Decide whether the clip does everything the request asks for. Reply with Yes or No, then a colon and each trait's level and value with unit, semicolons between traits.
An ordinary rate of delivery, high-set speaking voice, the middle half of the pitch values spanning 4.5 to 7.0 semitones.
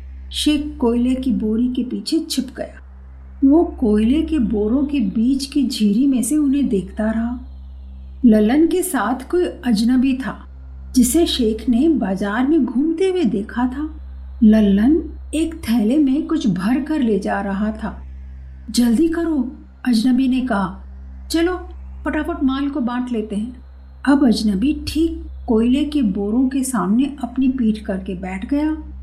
Yes: average, 150 wpm; high, 245 Hz; wide, 5.5 semitones